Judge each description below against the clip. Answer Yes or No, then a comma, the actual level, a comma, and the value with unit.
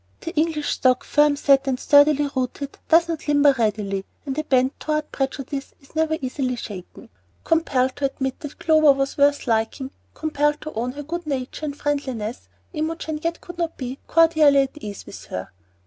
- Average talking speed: Yes, average, 180 wpm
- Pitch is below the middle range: No, very high, 285 Hz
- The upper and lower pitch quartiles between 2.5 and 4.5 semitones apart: Yes, average, 3.1 semitones